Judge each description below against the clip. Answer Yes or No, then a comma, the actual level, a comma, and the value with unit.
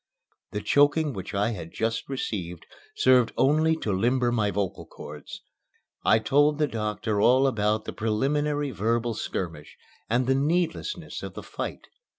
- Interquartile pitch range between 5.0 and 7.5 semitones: Yes, average, 5.3 semitones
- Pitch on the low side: Yes, low, 120 Hz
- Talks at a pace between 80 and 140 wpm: No, average, 150 wpm